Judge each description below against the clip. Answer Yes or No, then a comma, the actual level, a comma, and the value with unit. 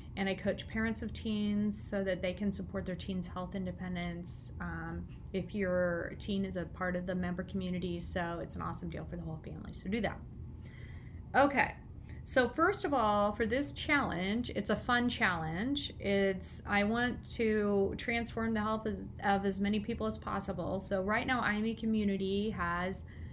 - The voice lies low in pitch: No, high, 195 Hz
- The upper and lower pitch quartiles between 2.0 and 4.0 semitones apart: Yes, average, 3.2 semitones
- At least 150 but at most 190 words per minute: Yes, average, 180 wpm